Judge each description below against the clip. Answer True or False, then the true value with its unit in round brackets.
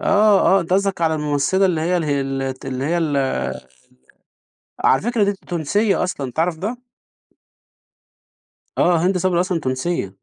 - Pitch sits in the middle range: True (170 Hz)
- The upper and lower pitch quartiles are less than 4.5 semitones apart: False (4.9 semitones)